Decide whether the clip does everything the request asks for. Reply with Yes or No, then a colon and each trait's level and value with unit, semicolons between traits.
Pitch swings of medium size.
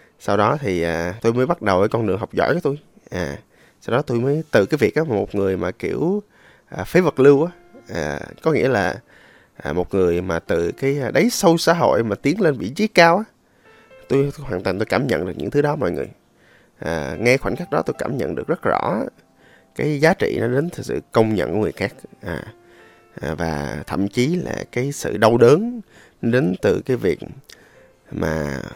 No: wide, 8.6 semitones